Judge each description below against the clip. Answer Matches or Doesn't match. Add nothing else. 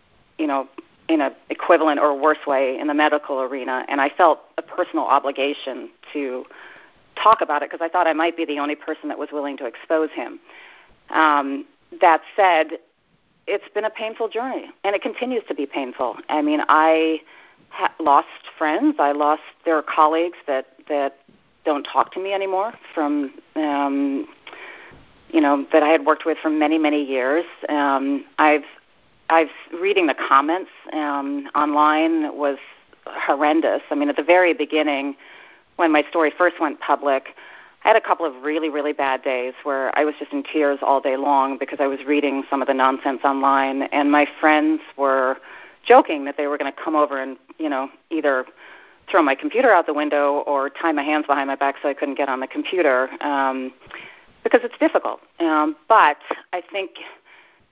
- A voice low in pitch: Doesn't match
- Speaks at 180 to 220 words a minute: Matches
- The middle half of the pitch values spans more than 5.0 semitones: Doesn't match